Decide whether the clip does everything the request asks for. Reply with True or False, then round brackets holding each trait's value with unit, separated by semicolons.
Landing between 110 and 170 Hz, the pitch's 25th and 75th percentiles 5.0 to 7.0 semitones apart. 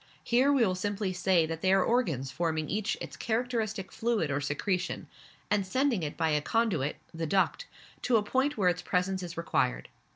False (190 Hz; 5.6 semitones)